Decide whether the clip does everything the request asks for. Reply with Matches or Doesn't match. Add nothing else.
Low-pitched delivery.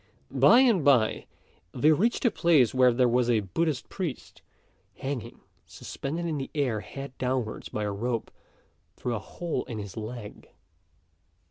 Matches